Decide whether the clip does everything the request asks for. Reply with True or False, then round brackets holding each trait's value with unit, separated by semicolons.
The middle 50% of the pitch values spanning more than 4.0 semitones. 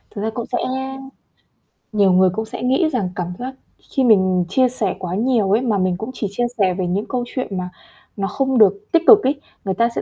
True (5.0 semitones)